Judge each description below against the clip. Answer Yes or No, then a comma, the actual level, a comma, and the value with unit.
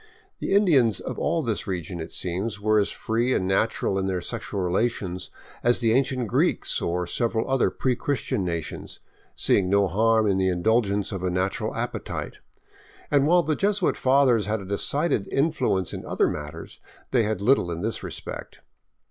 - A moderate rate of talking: Yes, average, 175 wpm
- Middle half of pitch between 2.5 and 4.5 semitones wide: No, average, 5.1 semitones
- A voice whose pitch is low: Yes, low, 110 Hz